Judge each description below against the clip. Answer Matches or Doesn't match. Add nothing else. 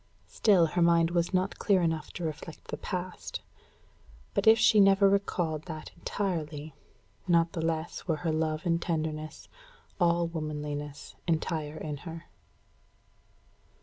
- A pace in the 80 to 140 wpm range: Matches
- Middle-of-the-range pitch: Matches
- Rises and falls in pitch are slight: Matches